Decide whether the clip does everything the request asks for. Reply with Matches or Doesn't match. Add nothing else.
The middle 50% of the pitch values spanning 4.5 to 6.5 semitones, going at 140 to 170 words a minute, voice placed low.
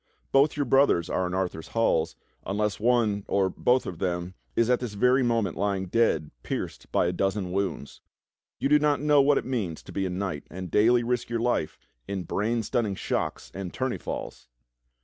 Doesn't match